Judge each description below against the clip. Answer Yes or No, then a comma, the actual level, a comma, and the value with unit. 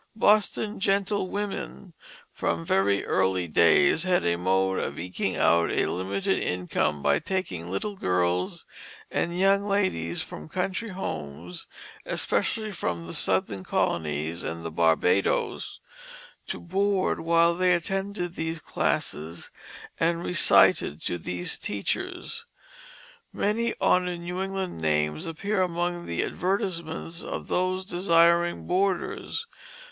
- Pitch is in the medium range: Yes, medium, 165 Hz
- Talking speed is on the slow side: Yes, slow, 115 wpm